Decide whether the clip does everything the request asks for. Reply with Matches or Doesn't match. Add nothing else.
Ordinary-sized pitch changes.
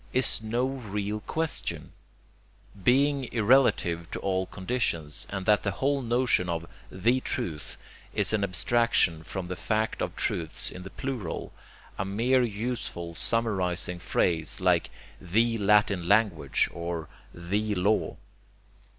Matches